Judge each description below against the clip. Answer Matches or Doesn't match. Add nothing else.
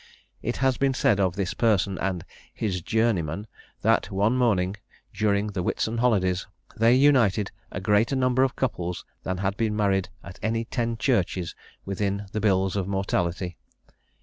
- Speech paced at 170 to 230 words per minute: Doesn't match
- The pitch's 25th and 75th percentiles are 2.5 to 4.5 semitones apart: Matches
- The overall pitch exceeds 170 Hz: Doesn't match